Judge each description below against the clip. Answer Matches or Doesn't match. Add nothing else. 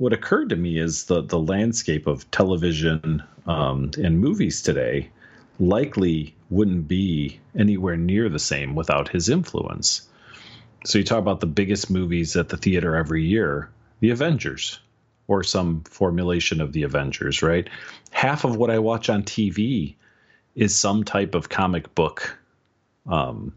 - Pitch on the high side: Doesn't match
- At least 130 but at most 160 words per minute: Matches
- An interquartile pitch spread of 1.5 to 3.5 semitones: Doesn't match